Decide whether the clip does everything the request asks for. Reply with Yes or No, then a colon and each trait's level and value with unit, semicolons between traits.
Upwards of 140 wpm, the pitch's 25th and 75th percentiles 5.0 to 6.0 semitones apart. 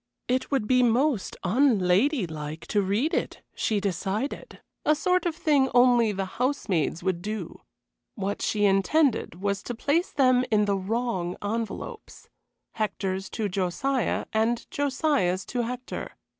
No: slow, 135 wpm; wide, 5.4 semitones